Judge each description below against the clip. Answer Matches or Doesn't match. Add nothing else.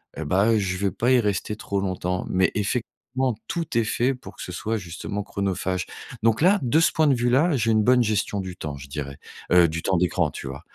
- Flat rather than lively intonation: Doesn't match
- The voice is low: Matches